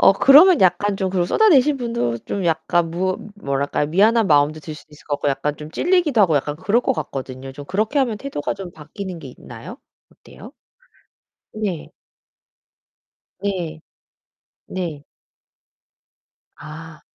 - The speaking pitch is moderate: Yes, medium, 175 Hz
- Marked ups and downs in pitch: Yes, wide, 6.1 semitones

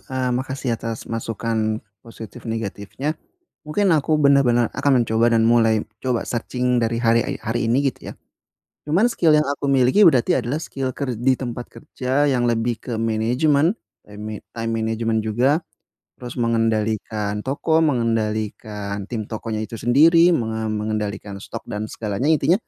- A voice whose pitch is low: Yes, low, 115 Hz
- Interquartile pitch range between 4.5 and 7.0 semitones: No, average, 3.4 semitones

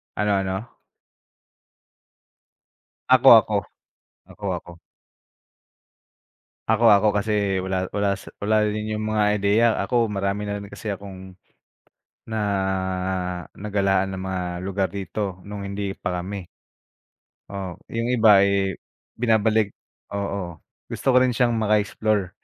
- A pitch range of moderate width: No, narrow, 1.8 semitones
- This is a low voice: Yes, low, 100 Hz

